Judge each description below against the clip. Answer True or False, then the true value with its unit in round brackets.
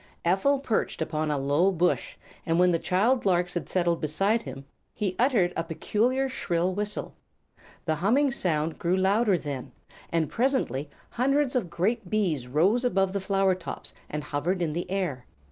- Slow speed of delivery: False (165 wpm)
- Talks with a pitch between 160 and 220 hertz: True (185 Hz)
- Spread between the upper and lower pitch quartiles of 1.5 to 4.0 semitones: False (4.8 semitones)